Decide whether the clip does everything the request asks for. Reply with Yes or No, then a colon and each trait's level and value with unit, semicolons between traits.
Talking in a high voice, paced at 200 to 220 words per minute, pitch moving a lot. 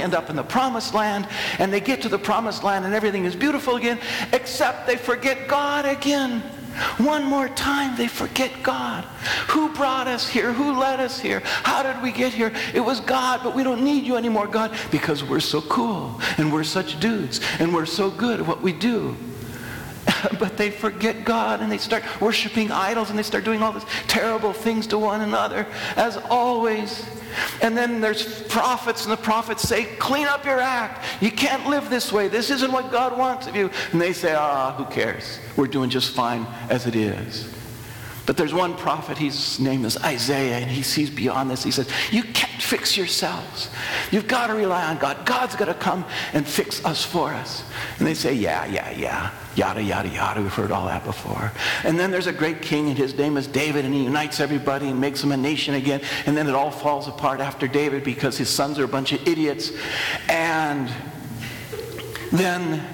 Yes: high, 195 Hz; fast, 205 wpm; wide, 9.0 semitones